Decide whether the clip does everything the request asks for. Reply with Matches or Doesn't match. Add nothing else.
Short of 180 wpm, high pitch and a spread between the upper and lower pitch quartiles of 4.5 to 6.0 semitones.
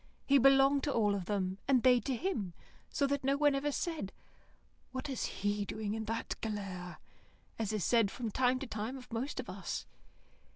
Doesn't match